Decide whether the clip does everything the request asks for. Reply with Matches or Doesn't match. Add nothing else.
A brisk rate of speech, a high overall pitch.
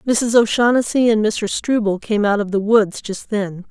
Doesn't match